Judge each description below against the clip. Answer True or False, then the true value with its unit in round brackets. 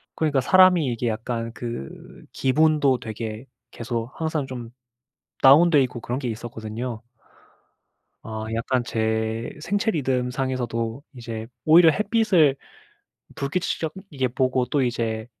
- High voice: False (125 Hz)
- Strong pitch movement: False (4.6 semitones)